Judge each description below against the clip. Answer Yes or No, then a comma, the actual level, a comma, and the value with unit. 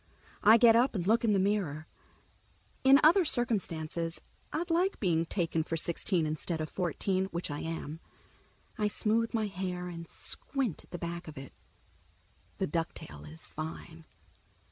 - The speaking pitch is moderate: Yes, medium, 180 Hz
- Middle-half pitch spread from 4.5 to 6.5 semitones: Yes, average, 5.2 semitones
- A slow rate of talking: No, average, 155 wpm